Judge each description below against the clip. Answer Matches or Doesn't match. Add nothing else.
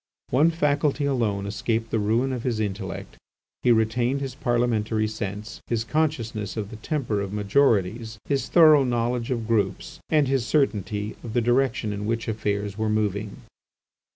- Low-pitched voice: Matches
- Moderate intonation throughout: Matches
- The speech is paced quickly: Doesn't match